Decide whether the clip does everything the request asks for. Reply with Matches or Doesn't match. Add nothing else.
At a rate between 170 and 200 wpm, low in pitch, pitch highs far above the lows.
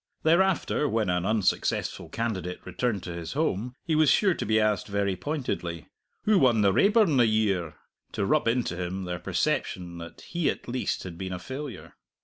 Matches